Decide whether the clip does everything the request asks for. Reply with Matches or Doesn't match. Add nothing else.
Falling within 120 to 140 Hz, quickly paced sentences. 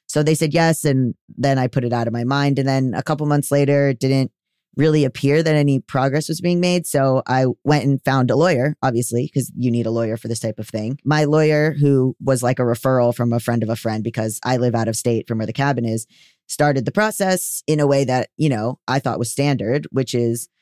Matches